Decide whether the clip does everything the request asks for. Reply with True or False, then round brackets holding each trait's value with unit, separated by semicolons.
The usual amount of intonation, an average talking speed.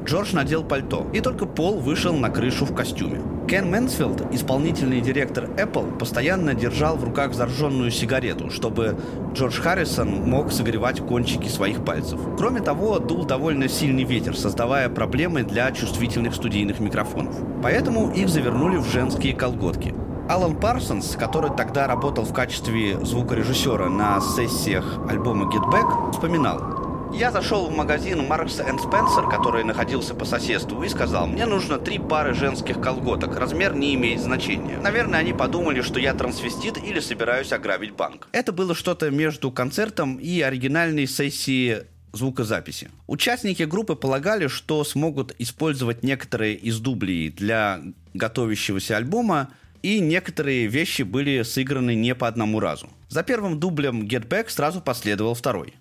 True (4.9 semitones; 140 wpm)